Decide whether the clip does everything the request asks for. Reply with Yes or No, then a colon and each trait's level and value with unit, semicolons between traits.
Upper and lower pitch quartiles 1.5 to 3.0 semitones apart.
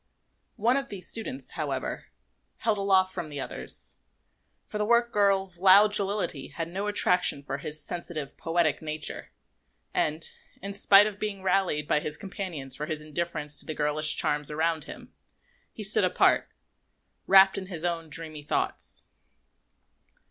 No: average, 4.6 semitones